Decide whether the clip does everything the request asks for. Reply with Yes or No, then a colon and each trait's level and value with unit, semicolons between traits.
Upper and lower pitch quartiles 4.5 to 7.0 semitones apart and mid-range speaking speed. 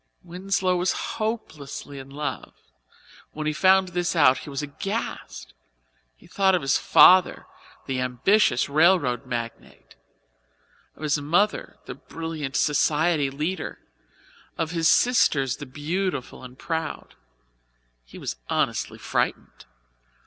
No: average, 5.0 semitones; slow, 120 wpm